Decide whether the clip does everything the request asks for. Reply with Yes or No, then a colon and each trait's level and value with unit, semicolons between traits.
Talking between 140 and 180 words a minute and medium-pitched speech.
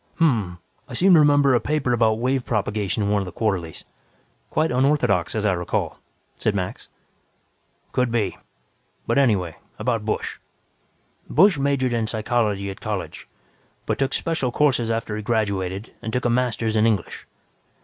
No: average, 165 wpm; low, 115 Hz